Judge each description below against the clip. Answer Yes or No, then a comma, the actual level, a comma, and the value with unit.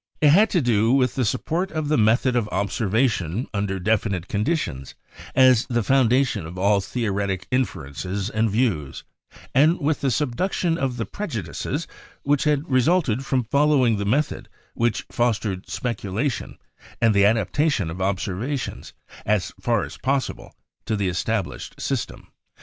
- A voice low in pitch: Yes, low, 115 Hz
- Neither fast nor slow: Yes, average, 150 wpm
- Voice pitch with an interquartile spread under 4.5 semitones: No, average, 5.3 semitones